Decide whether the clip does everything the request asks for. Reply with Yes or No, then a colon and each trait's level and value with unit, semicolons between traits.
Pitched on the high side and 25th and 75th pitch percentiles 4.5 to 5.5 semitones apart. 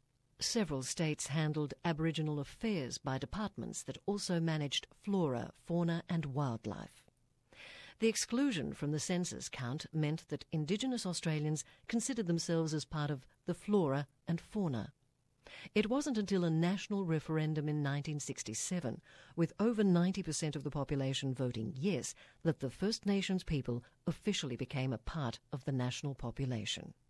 No: medium, 155 Hz; average, 5.0 semitones